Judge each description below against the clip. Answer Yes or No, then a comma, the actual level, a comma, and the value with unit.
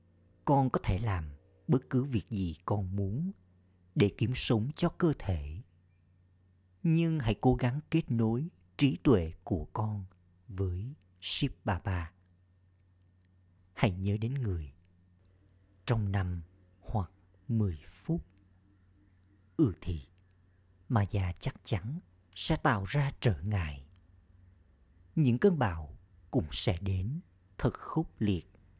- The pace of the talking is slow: Yes, slow, 120 wpm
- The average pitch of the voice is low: Yes, very low, 95 Hz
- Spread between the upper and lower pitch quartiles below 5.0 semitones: Yes, average, 4.5 semitones